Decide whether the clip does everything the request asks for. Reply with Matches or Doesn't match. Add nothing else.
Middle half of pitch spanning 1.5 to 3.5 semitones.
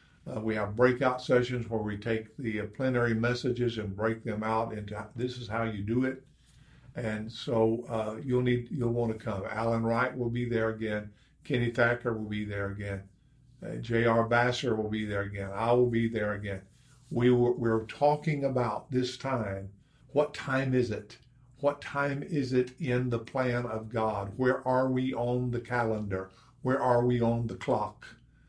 Matches